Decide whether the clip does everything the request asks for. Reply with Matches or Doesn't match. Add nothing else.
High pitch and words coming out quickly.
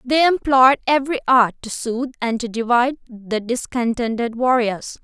Doesn't match